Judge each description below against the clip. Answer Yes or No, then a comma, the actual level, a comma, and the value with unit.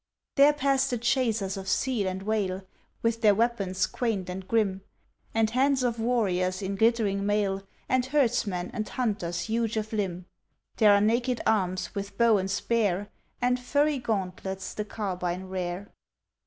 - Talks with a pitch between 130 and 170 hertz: No, high, 210 Hz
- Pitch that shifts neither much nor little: Yes, average, 3.7 semitones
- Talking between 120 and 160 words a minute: Yes, average, 155 wpm